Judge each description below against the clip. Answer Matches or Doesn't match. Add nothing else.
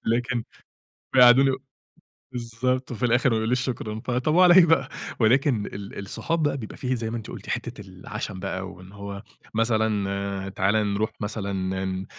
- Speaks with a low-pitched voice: Matches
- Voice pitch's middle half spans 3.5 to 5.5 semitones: Matches